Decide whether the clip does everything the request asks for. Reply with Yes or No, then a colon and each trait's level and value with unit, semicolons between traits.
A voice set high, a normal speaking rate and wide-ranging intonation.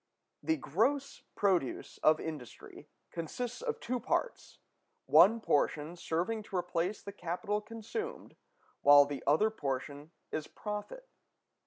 No: high, 195 Hz; slow, 120 wpm; wide, 6.7 semitones